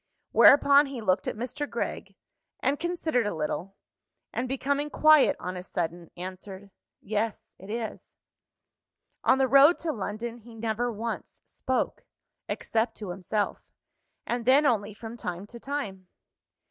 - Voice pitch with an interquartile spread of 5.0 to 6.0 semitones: Yes, wide, 5.5 semitones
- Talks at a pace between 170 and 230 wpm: No, average, 140 wpm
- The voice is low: No, high, 230 Hz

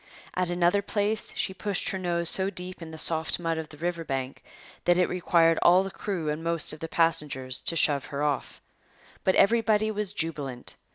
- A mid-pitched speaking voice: Yes, medium, 170 Hz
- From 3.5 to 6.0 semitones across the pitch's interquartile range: No, average, 3.1 semitones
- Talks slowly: No, average, 190 wpm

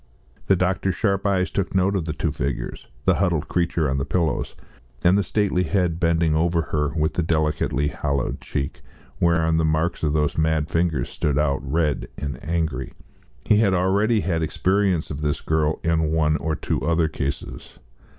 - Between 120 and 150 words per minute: No, average, 180 wpm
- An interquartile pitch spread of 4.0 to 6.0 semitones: No, average, 3.0 semitones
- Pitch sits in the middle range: No, very low, 80 Hz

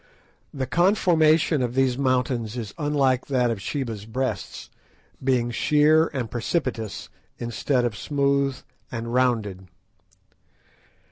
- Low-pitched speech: Yes, low, 130 Hz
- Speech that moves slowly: Yes, slow, 110 wpm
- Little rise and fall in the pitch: No, average, 3.3 semitones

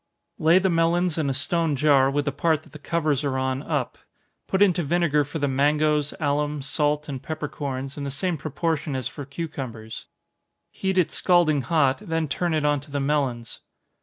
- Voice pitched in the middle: Yes, medium, 150 Hz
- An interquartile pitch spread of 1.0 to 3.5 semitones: Yes, average, 2.8 semitones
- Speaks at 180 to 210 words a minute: Yes, average, 190 wpm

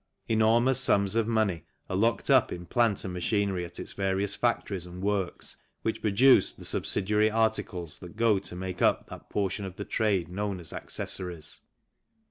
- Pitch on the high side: No, low, 100 Hz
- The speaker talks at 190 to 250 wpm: No, average, 170 wpm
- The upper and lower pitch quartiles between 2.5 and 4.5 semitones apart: Yes, average, 3.3 semitones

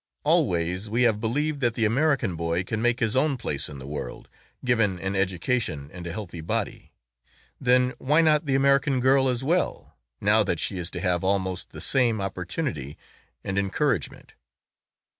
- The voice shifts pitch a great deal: Yes, wide, 6.5 semitones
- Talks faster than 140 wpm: Yes, average, 170 wpm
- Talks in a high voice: No, low, 110 Hz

